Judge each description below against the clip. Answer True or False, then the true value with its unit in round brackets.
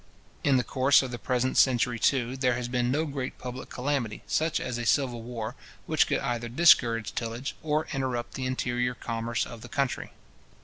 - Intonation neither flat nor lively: False (2.0 semitones)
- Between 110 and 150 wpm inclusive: False (185 wpm)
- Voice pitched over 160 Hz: False (125 Hz)